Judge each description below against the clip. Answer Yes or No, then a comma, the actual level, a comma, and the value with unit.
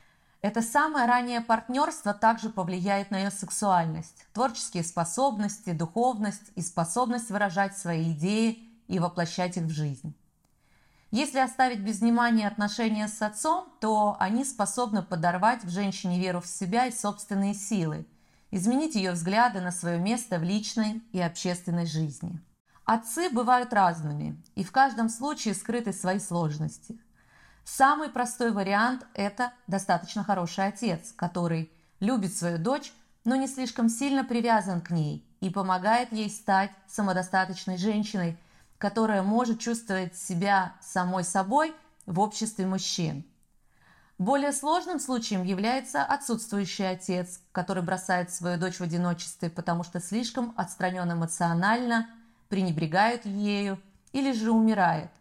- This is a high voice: Yes, high, 200 Hz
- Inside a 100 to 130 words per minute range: Yes, average, 125 wpm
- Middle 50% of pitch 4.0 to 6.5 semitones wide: Yes, average, 4.5 semitones